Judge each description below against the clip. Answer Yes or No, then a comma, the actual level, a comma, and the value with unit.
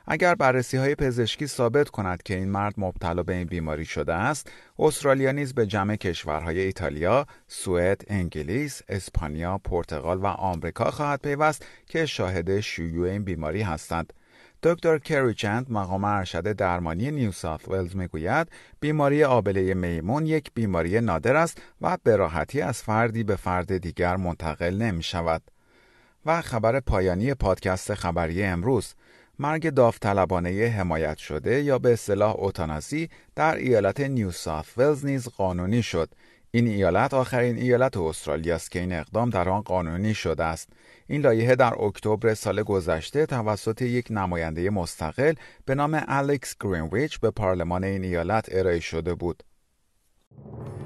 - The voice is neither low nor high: No, low, 100 Hz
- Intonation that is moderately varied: No, wide, 6.0 semitones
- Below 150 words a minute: Yes, average, 140 wpm